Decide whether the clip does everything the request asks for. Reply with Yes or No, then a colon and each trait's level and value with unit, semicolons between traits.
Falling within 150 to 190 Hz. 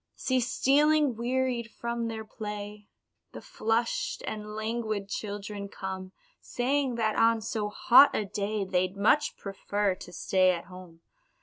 No: high, 215 Hz